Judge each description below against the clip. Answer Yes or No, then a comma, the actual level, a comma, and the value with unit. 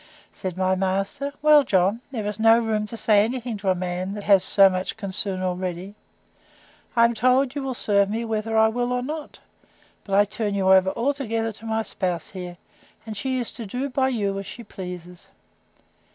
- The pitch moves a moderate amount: Yes, average, 3.8 semitones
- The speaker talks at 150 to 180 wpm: No, average, 200 wpm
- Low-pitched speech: No, high, 210 Hz